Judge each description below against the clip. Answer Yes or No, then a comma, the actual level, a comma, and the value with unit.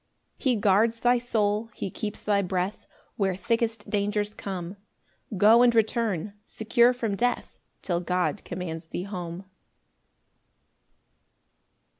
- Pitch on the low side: No, high, 205 Hz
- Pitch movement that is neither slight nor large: Yes, average, 3.6 semitones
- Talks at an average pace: No, slow, 120 wpm